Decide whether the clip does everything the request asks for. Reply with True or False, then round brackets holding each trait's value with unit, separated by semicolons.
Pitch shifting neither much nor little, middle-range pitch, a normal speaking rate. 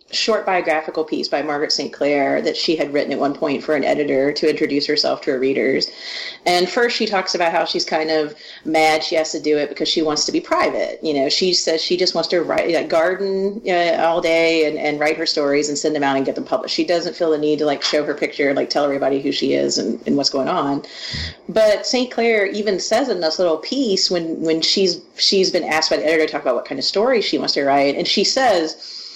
False (3.8 semitones; 165 Hz; 260 wpm)